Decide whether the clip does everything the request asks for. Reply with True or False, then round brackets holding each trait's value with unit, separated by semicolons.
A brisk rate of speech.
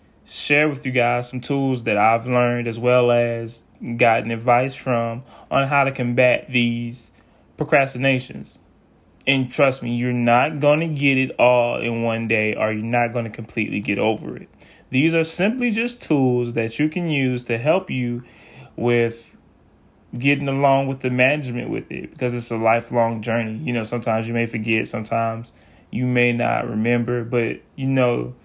False (175 wpm)